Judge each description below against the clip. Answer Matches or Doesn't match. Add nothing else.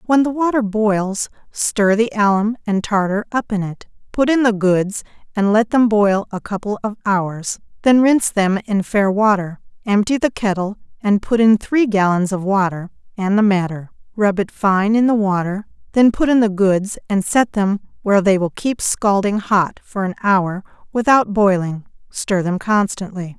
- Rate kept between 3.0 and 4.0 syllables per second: Doesn't match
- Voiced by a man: Doesn't match